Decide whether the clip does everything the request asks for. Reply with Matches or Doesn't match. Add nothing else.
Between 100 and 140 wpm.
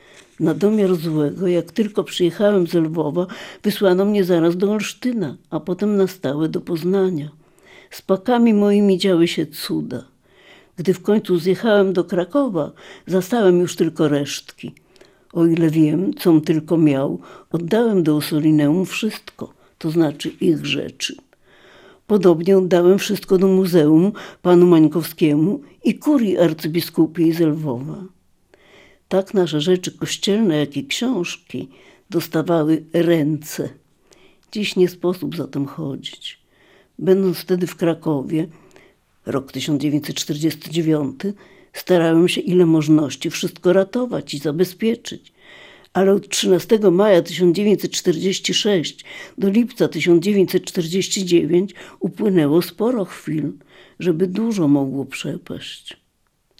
Matches